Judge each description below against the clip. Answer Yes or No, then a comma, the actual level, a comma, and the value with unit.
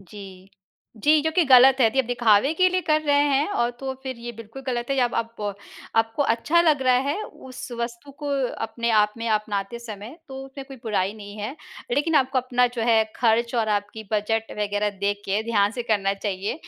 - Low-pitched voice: No, high, 235 Hz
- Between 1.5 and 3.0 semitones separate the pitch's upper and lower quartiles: No, average, 4.2 semitones